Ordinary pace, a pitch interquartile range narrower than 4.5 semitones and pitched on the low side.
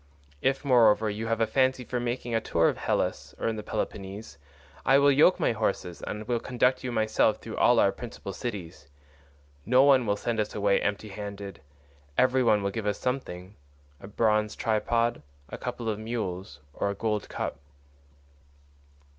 Yes: average, 170 wpm; average, 3.2 semitones; low, 110 Hz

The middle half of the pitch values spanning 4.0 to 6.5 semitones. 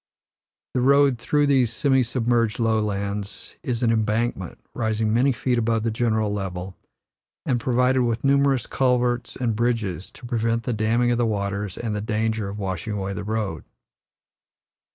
No: average, 2.7 semitones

